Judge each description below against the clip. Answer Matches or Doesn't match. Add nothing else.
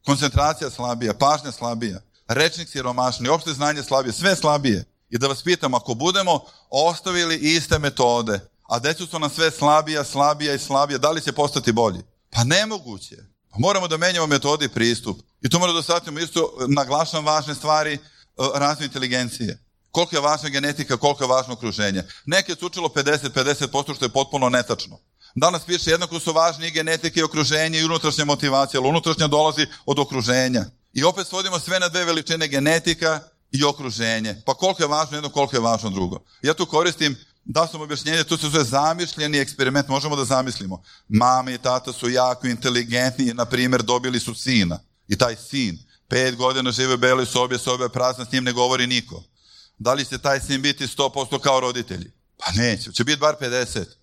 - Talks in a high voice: Doesn't match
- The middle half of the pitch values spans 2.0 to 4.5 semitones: Matches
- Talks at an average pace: Doesn't match